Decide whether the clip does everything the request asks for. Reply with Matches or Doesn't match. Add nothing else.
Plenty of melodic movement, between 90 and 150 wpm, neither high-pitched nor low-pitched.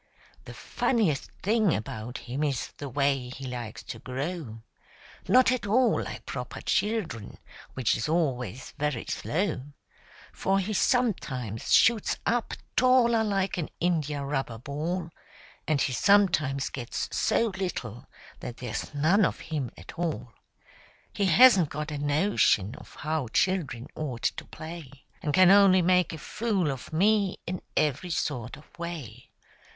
Matches